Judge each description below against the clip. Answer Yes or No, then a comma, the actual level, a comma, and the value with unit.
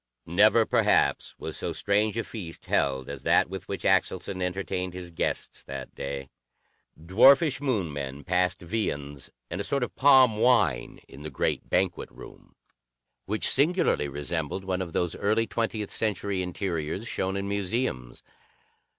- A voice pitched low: Yes, very low, 95 Hz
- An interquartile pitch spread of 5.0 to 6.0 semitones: Yes, wide, 5.5 semitones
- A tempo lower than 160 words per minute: Yes, average, 150 wpm